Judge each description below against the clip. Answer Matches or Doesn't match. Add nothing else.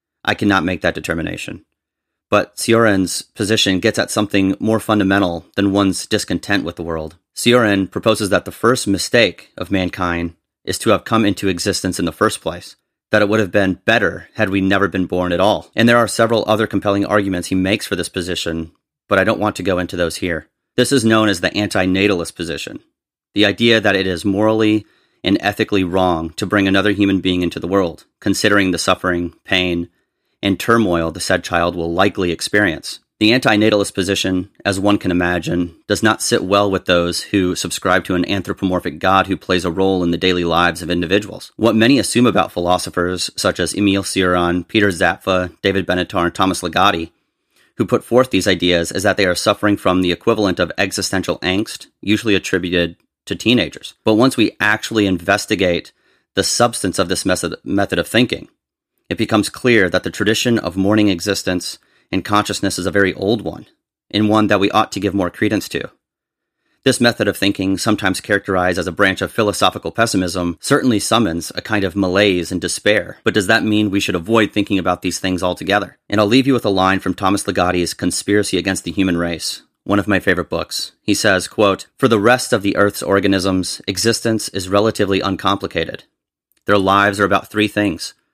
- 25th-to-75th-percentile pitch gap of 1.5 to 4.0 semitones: Matches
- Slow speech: Doesn't match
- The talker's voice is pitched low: Matches